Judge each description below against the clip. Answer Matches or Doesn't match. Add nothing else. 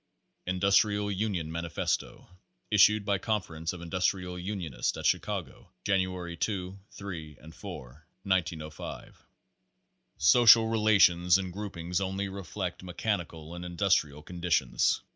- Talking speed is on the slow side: Matches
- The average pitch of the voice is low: Matches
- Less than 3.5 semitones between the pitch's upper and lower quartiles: Matches